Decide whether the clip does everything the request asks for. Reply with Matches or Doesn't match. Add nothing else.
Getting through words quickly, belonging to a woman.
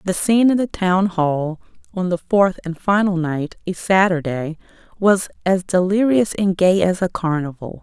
Doesn't match